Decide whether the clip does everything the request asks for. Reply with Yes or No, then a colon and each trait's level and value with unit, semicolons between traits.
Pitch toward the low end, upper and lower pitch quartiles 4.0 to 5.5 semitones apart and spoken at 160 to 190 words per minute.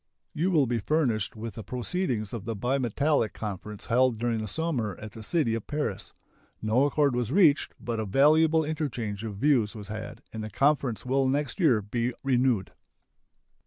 Yes: low, 120 Hz; average, 4.9 semitones; average, 175 wpm